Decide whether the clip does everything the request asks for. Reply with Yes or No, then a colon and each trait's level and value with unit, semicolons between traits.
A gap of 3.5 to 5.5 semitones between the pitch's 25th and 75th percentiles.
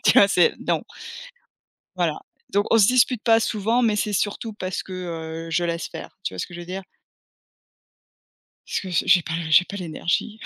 Yes: average, 4.0 semitones